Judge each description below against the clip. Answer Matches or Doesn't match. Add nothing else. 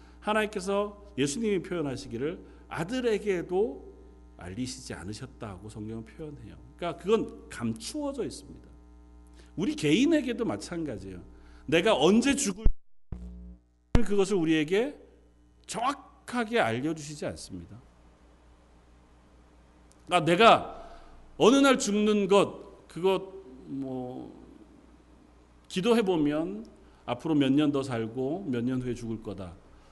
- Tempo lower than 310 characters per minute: Matches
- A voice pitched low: Matches